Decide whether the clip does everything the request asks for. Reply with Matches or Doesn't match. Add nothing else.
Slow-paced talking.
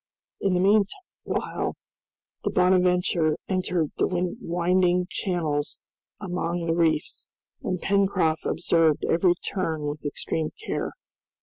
Matches